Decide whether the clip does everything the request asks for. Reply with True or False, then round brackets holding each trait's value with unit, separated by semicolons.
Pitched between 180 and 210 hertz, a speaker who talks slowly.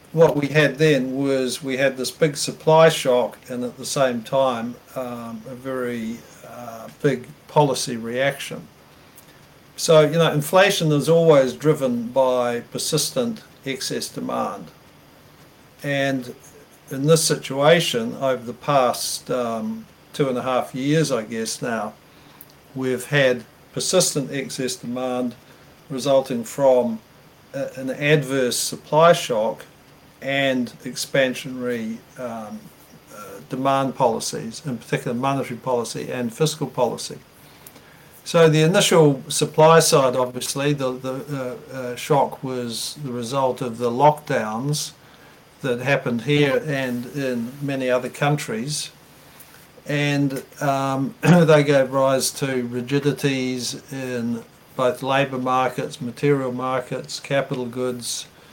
False (135 Hz; 120 wpm)